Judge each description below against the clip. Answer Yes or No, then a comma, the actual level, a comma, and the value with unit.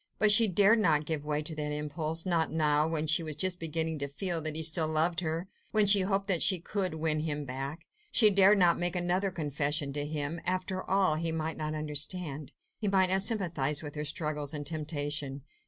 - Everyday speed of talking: No, fast, 210 wpm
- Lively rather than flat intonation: No, average, 3.6 semitones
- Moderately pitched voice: Yes, medium, 160 Hz